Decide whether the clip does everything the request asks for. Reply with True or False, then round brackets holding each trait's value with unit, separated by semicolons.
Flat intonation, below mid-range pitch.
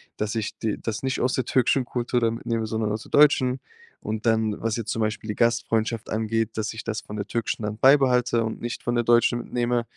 True (1.7 semitones; 115 Hz)